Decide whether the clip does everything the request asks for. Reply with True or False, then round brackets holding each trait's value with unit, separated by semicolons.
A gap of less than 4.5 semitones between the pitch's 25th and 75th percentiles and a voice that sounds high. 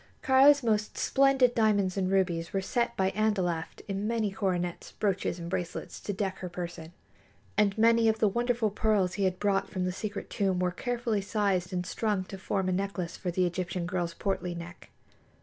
True (3.0 semitones; 195 Hz)